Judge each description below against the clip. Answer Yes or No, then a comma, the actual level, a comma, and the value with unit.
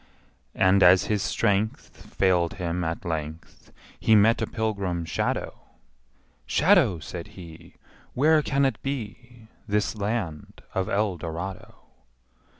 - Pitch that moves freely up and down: No, average, 4.3 semitones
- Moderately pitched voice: No, low, 100 Hz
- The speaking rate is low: Yes, slow, 115 wpm